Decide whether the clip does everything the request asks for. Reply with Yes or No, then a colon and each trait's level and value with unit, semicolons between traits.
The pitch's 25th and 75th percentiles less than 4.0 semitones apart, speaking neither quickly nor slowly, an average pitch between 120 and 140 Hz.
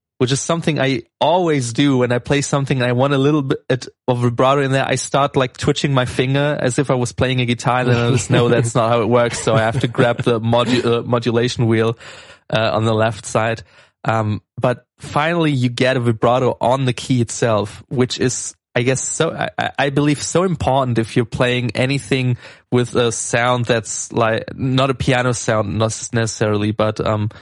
No: narrow, 2.4 semitones; fast, 210 wpm; low, 125 Hz